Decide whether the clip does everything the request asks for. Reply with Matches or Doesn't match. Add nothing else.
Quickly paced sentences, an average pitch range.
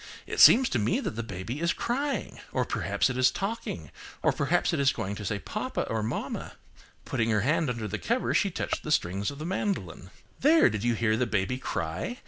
Doesn't match